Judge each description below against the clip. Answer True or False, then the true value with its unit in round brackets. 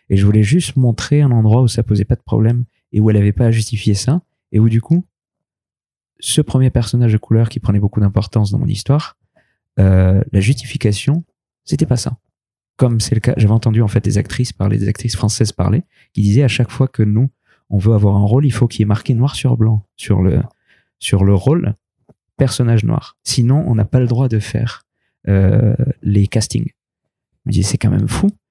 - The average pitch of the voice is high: False (115 Hz)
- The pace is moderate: False (225 wpm)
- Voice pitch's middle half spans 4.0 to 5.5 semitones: False (3.5 semitones)